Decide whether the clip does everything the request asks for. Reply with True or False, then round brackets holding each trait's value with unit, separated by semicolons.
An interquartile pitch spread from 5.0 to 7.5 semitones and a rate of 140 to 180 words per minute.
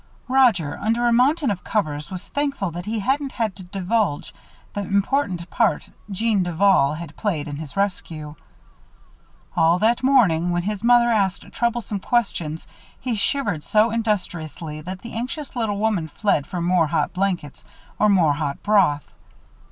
True (5.3 semitones; 155 wpm)